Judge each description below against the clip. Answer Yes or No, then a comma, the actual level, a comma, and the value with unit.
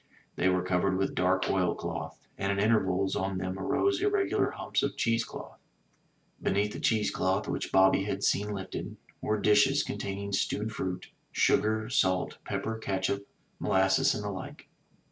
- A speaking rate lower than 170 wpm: Yes, average, 160 wpm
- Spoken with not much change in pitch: Yes, narrow, 2.2 semitones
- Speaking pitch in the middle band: No, low, 100 Hz